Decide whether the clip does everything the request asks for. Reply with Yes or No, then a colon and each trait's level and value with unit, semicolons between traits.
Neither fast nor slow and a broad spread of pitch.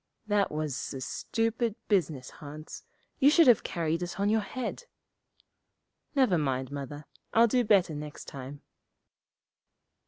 No: slow, 130 wpm; wide, 7.5 semitones